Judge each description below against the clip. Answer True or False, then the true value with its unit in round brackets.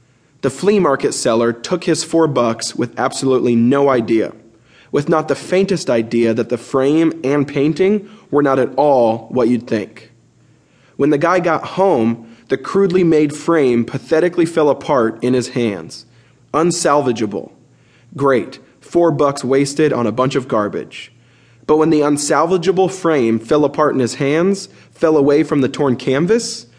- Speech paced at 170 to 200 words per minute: False (155 wpm)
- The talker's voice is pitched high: False (140 Hz)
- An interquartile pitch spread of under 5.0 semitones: False (5.4 semitones)